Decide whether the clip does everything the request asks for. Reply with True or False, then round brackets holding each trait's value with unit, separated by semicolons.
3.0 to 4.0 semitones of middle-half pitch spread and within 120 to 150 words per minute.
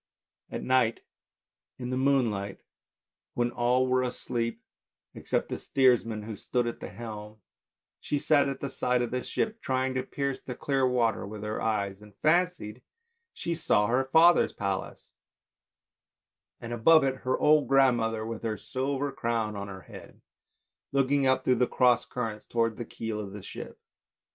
False (3.3 semitones; 170 wpm)